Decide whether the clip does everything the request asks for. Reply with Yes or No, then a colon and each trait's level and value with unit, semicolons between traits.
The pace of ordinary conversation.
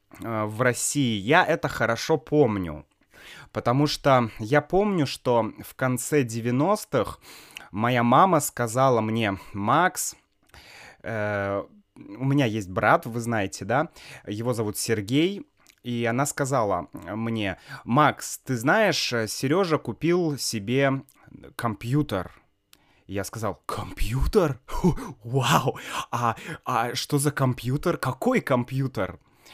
No: slow, 105 wpm